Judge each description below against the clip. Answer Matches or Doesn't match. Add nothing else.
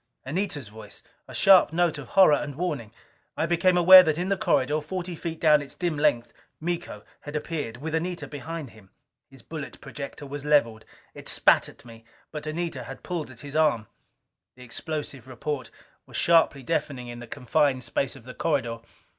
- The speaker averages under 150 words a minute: Doesn't match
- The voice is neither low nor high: Matches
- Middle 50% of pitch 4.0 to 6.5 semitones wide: Matches